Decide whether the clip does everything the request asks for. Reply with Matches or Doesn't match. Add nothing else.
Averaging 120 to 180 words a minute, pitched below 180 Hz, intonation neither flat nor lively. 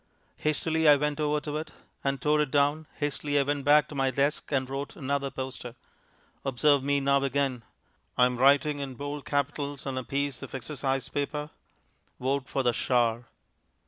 Doesn't match